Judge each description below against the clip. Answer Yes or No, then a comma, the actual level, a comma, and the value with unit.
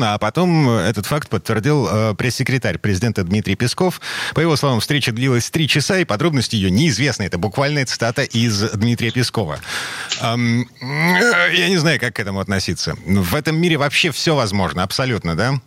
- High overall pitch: No, low, 120 Hz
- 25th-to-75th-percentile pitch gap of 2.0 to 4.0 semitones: No, average, 5.2 semitones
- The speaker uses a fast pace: Yes, fast, 165 wpm